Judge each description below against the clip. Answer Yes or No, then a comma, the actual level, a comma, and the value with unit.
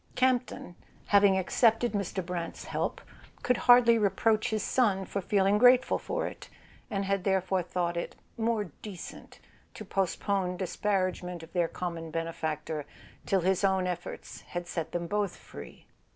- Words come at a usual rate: Yes, average, 145 wpm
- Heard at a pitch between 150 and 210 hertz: Yes, high, 190 Hz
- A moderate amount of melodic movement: Yes, average, 3.0 semitones